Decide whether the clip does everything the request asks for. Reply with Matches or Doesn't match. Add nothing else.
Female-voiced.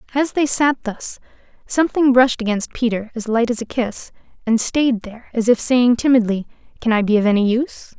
Matches